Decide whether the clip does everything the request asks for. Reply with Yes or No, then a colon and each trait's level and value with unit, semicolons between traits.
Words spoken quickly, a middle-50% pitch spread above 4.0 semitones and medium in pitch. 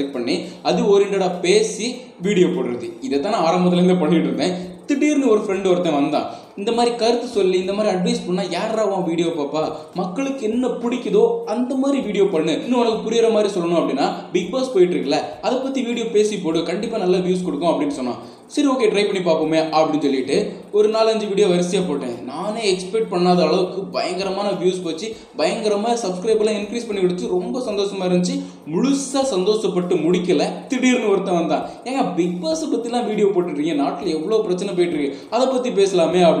No: fast, 170 wpm; average, 4.5 semitones; high, 200 Hz